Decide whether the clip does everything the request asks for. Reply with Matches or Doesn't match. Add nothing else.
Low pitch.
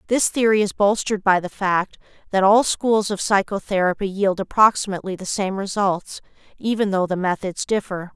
Doesn't match